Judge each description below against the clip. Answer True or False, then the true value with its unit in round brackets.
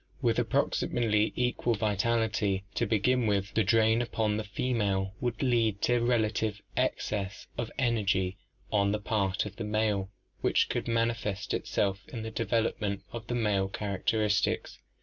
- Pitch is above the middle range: False (110 Hz)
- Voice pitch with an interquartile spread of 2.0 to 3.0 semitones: True (2.5 semitones)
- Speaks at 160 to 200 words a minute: False (150 wpm)